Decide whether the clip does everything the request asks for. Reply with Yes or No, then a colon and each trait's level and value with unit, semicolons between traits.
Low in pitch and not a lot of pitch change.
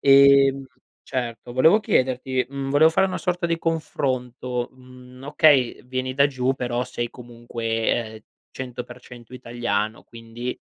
Yes: low, 125 Hz; narrow, 2.3 semitones